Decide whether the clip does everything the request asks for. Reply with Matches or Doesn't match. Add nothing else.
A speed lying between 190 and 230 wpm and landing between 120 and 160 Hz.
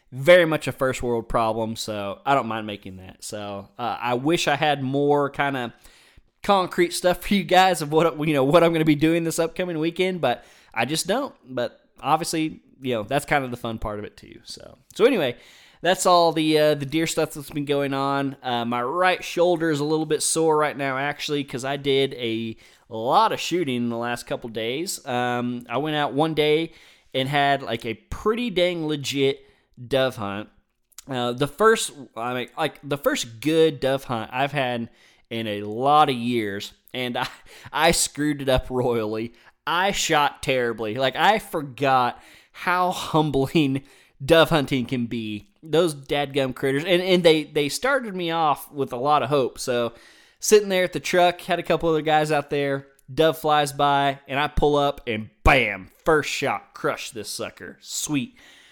Matches